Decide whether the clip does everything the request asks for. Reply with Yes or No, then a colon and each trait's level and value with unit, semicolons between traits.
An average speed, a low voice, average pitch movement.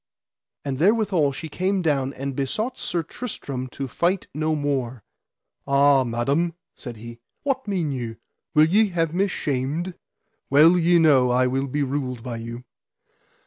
No: average, 150 wpm; medium, 145 Hz; average, 5.0 semitones